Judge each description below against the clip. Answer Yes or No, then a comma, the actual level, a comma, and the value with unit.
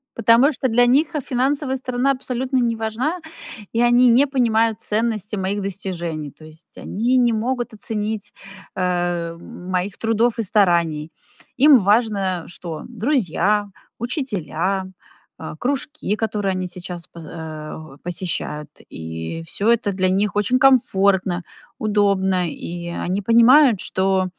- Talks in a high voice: Yes, high, 205 Hz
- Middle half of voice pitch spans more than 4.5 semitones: Yes, average, 5.1 semitones